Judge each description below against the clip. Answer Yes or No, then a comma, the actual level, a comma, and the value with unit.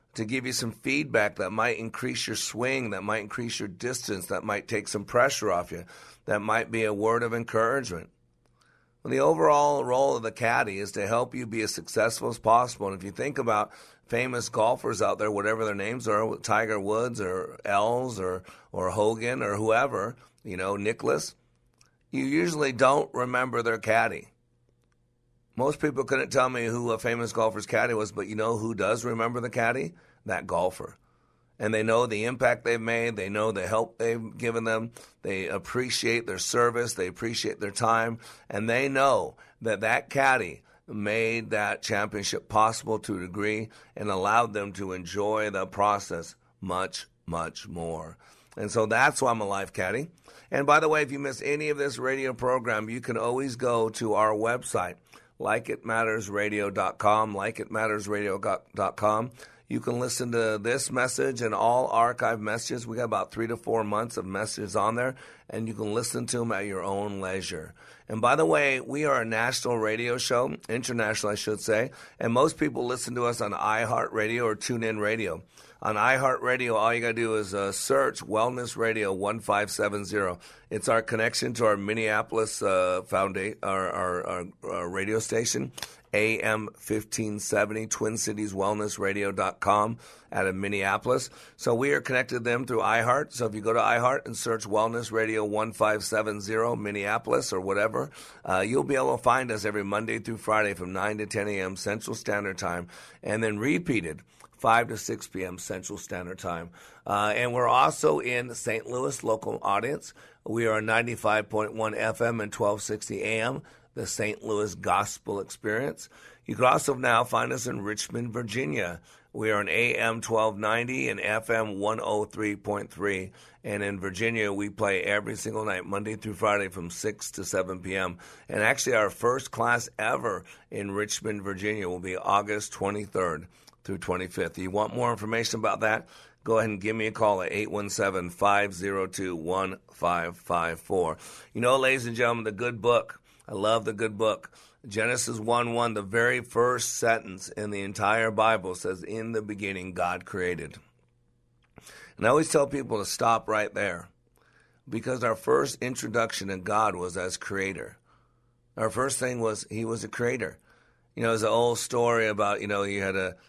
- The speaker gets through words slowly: No, average, 180 wpm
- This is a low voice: Yes, low, 110 Hz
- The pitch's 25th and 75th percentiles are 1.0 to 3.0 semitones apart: Yes, narrow, 2.5 semitones